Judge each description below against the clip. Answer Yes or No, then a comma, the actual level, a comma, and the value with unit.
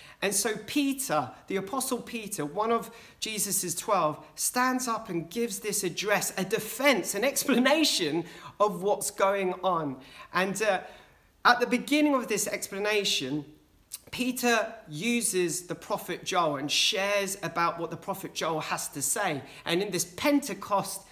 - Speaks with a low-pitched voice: No, high, 195 Hz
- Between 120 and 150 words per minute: Yes, average, 145 wpm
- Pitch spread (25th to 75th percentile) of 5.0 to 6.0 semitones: Yes, wide, 5.6 semitones